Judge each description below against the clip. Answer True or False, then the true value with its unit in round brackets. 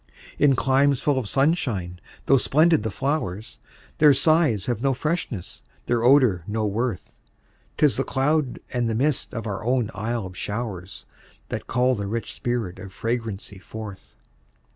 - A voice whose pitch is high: False (120 Hz)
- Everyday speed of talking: True (155 wpm)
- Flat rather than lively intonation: False (4.7 semitones)